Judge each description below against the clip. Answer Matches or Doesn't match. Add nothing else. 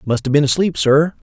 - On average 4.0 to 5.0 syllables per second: Doesn't match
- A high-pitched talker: Doesn't match